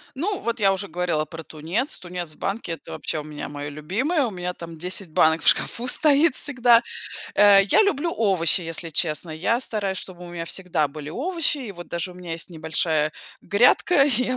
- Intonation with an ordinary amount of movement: No, wide, 6.6 semitones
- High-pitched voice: No, medium, 180 Hz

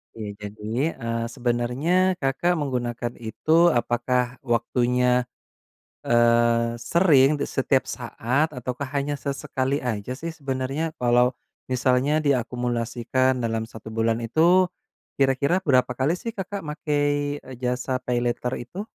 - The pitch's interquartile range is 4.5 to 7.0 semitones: No, average, 3.3 semitones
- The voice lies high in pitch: No, low, 130 Hz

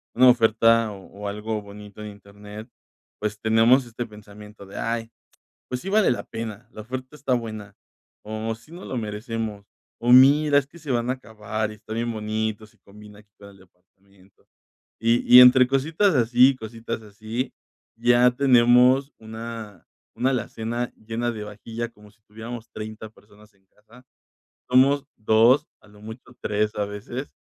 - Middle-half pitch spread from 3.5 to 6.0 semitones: No, average, 2.8 semitones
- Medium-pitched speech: No, low, 110 Hz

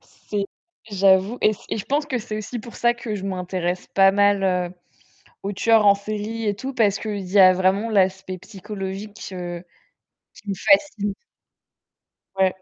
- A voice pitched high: Yes, high, 200 Hz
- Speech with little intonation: Yes, narrow, 2.2 semitones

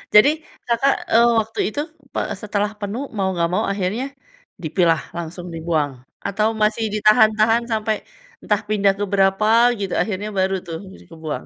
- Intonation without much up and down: No, average, 3.0 semitones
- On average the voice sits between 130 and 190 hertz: No, high, 205 Hz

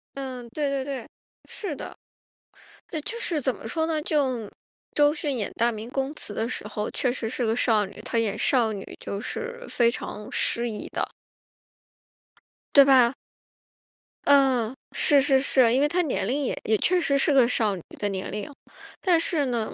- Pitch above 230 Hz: Yes, very high, 255 Hz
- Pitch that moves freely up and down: No, average, 4.4 semitones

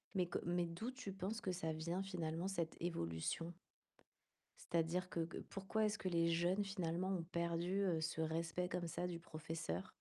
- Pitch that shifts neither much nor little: No, narrow, 2.1 semitones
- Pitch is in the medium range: Yes, medium, 175 Hz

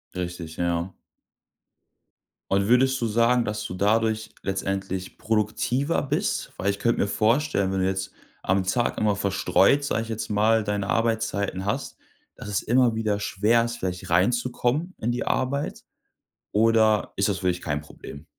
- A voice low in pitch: Yes, low, 105 Hz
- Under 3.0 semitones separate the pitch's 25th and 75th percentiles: No, average, 3.5 semitones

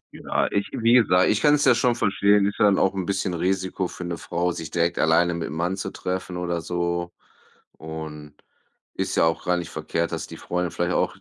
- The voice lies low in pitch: Yes, very low, 90 Hz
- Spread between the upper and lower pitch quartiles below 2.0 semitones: No, narrow, 2.5 semitones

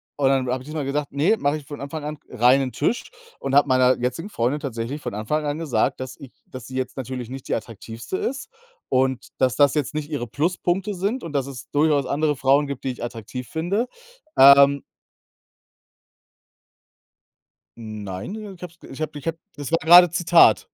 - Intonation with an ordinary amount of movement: Yes, average, 3.4 semitones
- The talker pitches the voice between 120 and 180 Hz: Yes, medium, 140 Hz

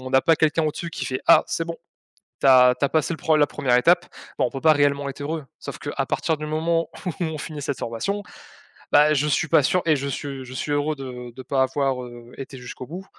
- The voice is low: No, medium, 145 Hz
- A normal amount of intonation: Yes, average, 3.2 semitones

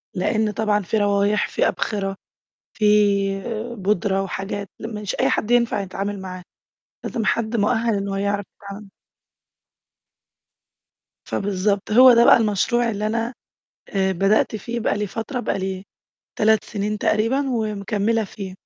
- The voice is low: No, high, 210 Hz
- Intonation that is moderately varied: No, narrow, 2.1 semitones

